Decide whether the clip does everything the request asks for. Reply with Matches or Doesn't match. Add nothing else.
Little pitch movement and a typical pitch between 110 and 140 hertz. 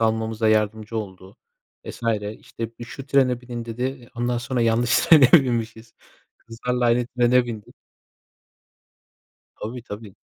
Matches